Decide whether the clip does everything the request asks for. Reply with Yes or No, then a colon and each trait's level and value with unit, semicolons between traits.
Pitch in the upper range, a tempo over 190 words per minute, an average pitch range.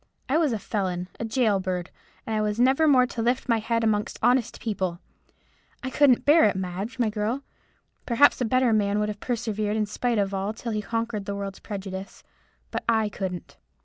Yes: high, 215 Hz; average, 200 wpm; average, 3.3 semitones